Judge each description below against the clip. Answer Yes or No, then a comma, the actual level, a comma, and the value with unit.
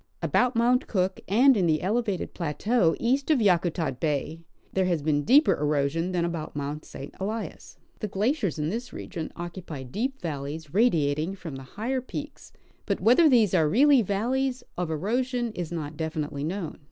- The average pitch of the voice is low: No, medium, 185 Hz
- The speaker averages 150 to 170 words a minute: Yes, average, 165 wpm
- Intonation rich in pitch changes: Yes, wide, 7.4 semitones